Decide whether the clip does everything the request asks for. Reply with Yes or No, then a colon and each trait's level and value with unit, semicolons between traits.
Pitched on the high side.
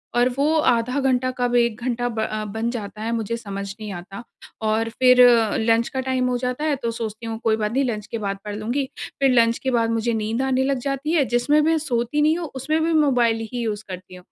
Yes: high, 235 Hz